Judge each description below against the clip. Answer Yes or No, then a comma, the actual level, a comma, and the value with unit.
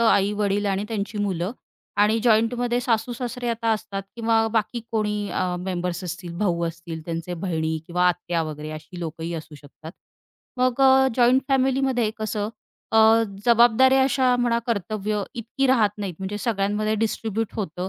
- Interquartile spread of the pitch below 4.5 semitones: No, average, 4.8 semitones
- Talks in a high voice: Yes, high, 210 Hz